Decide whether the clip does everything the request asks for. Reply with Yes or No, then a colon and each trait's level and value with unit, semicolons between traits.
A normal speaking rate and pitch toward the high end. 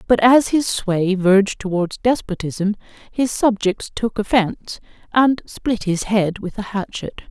Yes: average, 150 wpm; high, 210 Hz